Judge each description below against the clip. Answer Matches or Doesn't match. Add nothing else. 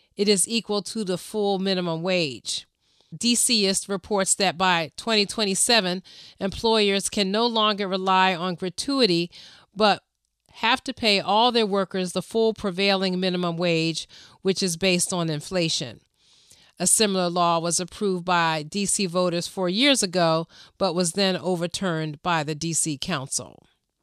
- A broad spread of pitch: Doesn't match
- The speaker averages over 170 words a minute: Doesn't match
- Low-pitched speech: Doesn't match